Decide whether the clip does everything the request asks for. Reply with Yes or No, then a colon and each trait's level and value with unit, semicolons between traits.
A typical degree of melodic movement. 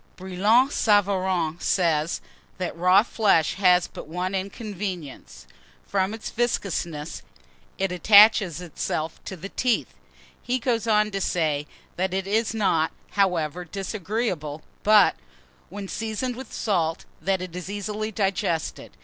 Yes: average, 3.5 semitones